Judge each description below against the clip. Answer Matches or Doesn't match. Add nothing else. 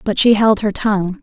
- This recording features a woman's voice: Matches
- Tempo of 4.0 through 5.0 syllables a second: Doesn't match